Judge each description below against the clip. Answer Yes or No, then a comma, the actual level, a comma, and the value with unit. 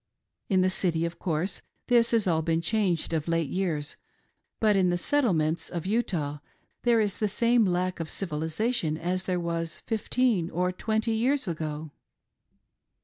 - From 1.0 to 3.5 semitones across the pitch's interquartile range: No, average, 4.9 semitones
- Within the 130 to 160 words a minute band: Yes, average, 155 wpm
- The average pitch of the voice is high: No, medium, 180 Hz